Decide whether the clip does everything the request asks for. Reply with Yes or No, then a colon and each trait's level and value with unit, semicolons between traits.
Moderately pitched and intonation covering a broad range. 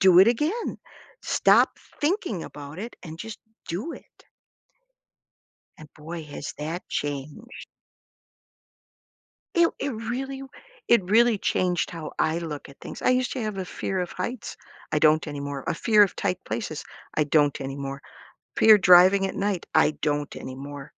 Yes: medium, 180 Hz; wide, 6.8 semitones